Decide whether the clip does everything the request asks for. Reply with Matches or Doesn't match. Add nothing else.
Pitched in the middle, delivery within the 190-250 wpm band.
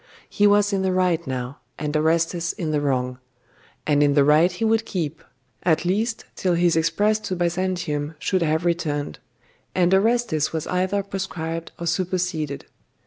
Doesn't match